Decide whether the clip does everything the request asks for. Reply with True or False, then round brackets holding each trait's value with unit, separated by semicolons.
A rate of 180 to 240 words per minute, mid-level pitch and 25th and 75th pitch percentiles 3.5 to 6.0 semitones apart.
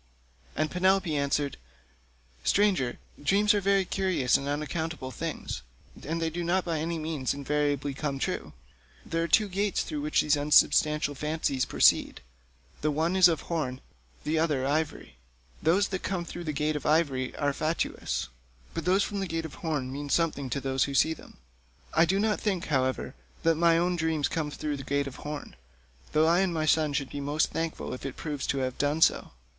False (195 wpm; 155 Hz; 3.0 semitones)